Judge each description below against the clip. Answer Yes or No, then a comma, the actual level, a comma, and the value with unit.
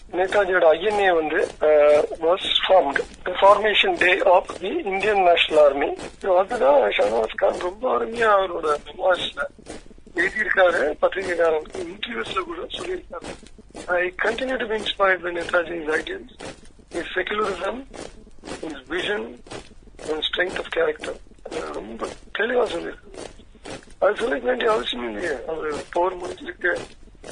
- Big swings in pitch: Yes, wide, 5.7 semitones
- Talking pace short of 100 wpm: Yes, average, 80 wpm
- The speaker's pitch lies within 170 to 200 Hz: Yes, high, 195 Hz